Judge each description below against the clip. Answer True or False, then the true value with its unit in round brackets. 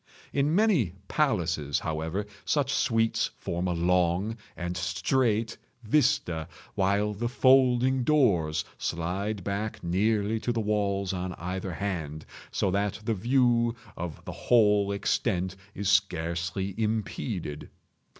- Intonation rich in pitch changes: False (4.4 semitones)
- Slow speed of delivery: True (120 wpm)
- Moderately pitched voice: False (100 Hz)